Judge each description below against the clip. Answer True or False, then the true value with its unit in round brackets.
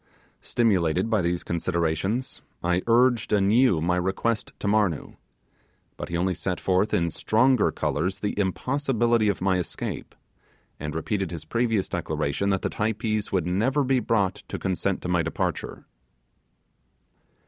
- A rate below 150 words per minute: True (140 wpm)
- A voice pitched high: False (95 Hz)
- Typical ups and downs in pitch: True (4.3 semitones)